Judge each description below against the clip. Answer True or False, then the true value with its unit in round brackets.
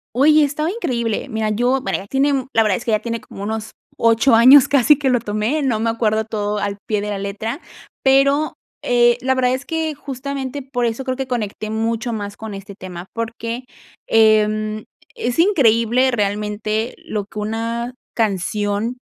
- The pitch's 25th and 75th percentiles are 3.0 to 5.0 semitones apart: True (3.6 semitones)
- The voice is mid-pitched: False (230 Hz)